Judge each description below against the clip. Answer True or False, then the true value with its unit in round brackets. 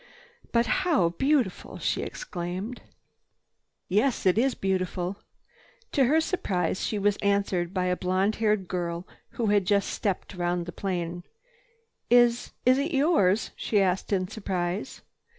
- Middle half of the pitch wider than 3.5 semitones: True (4.4 semitones)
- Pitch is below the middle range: False (195 Hz)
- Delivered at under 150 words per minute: True (135 wpm)